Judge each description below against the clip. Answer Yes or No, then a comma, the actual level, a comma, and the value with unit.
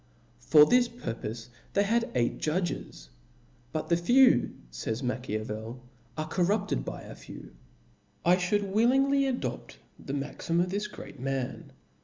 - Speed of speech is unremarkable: Yes, average, 155 wpm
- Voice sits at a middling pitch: Yes, medium, 170 Hz